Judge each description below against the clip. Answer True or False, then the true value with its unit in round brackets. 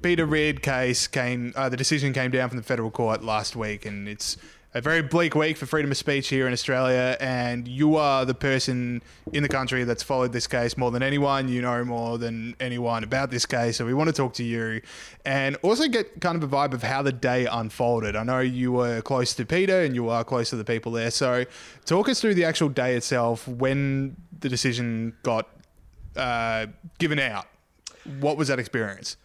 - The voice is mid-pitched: False (130 Hz)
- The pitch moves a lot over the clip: False (2.8 semitones)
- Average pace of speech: False (215 wpm)